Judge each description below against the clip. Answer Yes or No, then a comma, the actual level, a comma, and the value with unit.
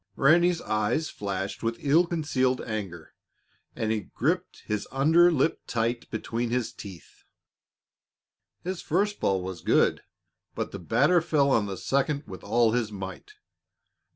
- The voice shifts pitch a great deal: Yes, wide, 7.0 semitones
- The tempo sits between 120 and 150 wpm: Yes, average, 140 wpm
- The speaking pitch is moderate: No, low, 120 Hz